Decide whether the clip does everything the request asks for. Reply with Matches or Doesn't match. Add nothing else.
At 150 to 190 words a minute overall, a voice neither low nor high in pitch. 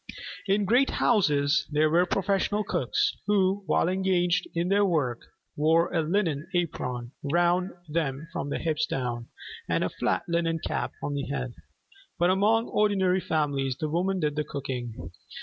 Matches